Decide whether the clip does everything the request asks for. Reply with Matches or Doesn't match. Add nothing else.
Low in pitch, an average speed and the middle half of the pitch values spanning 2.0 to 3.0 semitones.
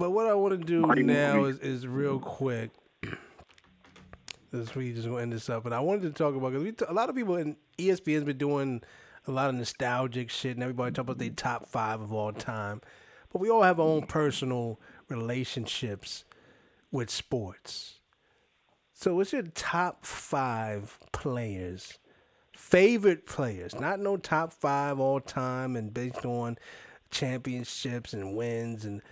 Doesn't match